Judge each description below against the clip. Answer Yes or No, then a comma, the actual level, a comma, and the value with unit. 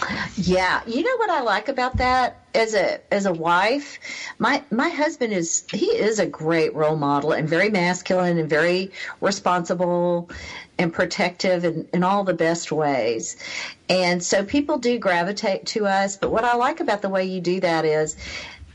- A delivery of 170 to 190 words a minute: Yes, average, 175 wpm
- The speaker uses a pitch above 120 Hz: Yes, medium, 185 Hz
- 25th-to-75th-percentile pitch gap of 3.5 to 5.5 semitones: Yes, average, 3.8 semitones